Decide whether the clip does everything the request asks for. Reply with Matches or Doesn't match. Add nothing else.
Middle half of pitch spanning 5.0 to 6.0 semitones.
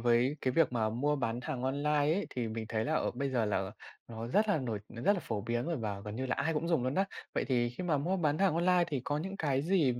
Matches